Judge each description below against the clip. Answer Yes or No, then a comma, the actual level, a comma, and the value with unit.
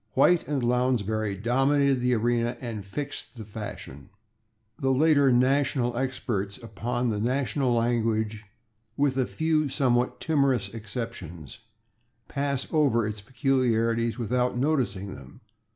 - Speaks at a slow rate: Yes, slow, 120 wpm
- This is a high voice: No, low, 120 Hz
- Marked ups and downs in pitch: No, average, 3.4 semitones